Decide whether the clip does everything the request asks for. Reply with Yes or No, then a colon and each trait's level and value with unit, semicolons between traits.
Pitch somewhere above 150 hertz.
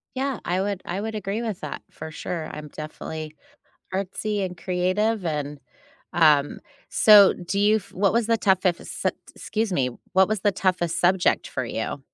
Yes: medium, 185 Hz